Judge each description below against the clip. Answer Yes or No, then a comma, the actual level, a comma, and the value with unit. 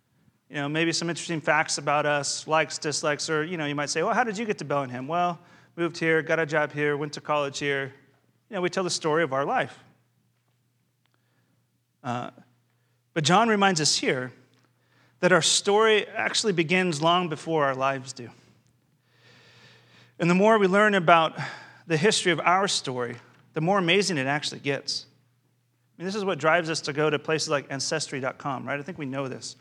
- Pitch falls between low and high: Yes, medium, 155 Hz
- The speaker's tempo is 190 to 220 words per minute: Yes, average, 195 wpm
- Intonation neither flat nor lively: Yes, average, 4.1 semitones